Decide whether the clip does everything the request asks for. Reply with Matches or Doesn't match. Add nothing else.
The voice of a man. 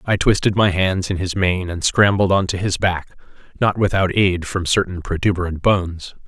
Matches